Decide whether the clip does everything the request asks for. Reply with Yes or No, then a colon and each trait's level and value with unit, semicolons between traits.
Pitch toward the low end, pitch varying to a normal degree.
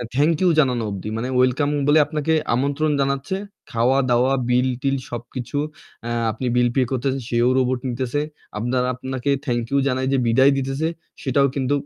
No: low, 130 Hz; narrow, 2.0 semitones